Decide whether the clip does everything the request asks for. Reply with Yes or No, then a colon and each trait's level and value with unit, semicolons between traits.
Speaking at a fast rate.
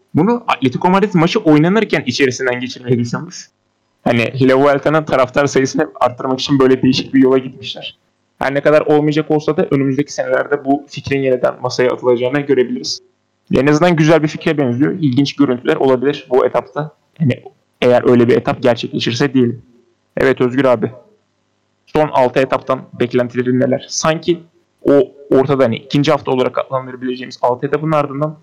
Yes: fast, 150 wpm